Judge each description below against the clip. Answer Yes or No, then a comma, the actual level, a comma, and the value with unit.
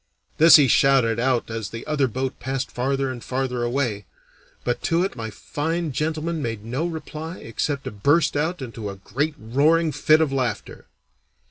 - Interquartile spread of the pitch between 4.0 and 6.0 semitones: Yes, average, 4.5 semitones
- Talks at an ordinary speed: Yes, average, 170 wpm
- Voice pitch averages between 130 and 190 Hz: Yes, low, 135 Hz